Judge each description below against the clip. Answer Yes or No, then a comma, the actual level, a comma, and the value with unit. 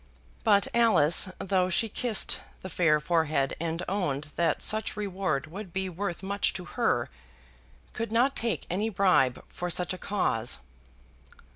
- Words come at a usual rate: Yes, average, 145 wpm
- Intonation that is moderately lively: Yes, average, 4.2 semitones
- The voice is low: No, medium, 185 Hz